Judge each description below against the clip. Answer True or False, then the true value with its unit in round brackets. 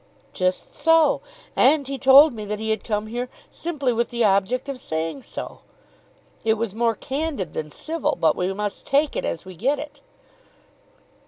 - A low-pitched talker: False (235 Hz)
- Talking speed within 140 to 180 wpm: True (175 wpm)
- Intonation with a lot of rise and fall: True (5.8 semitones)